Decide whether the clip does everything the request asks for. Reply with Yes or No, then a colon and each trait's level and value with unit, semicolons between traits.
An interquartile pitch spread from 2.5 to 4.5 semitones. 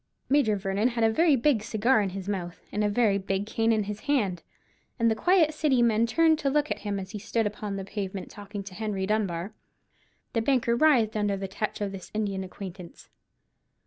Yes: average, 3.1 semitones